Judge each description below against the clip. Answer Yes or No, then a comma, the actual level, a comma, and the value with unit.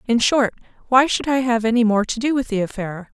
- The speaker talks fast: Yes, fast, 245 wpm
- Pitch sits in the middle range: No, high, 235 Hz